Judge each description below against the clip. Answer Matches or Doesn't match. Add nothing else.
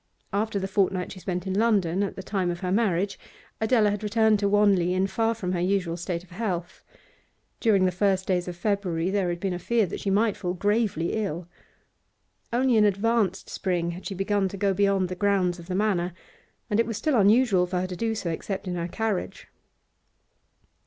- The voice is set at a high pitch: Matches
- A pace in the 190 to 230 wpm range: Matches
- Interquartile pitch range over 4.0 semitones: Doesn't match